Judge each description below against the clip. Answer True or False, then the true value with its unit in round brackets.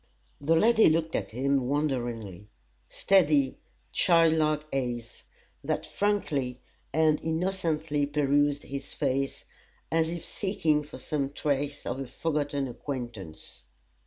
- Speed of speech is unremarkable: False (115 wpm)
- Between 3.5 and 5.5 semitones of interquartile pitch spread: False (3.1 semitones)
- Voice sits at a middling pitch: True (145 Hz)